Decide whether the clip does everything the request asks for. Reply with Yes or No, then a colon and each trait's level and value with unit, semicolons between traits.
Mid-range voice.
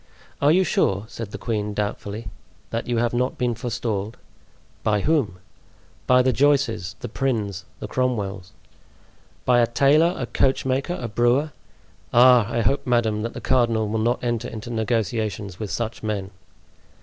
No: low, 115 Hz